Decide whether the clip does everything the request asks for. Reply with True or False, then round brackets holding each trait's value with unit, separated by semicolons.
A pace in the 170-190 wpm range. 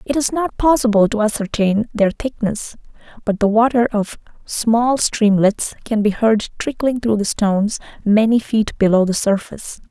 False (155 wpm)